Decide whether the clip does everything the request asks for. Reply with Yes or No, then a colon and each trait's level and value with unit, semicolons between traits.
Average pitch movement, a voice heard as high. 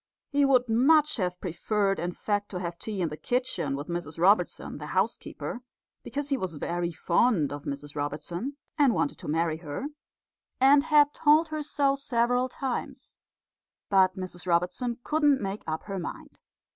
No: wide, 7.7 semitones; high, 195 Hz